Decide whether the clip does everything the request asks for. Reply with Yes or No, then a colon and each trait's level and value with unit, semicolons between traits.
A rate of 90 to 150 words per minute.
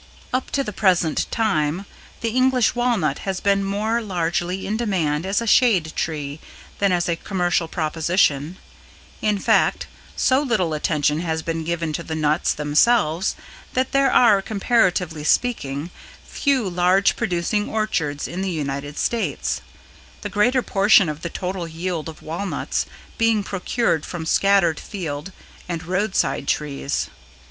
Yes: average, 140 wpm